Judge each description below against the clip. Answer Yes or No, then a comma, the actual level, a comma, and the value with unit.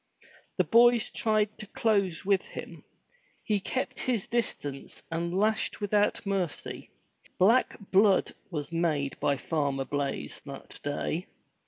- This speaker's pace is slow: Yes, slow, 125 wpm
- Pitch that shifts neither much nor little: No, wide, 6.2 semitones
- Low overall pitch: No, high, 190 Hz